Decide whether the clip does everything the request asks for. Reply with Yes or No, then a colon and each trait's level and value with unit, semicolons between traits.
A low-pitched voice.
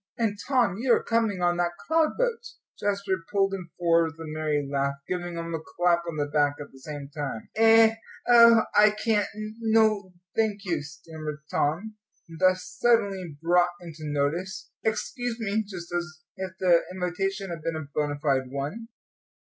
No: medium, 180 Hz